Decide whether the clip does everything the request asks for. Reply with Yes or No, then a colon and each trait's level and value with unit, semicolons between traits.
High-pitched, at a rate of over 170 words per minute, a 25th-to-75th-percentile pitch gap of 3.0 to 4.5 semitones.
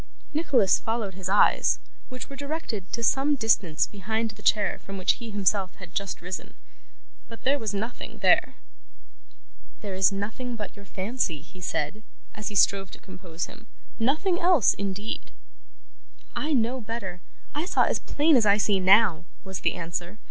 No: high, 210 Hz; average, 165 wpm; average, 4.2 semitones